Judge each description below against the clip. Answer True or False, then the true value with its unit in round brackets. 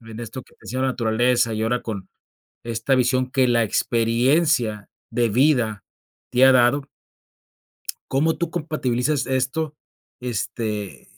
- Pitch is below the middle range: True (125 Hz)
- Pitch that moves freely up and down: False (2.8 semitones)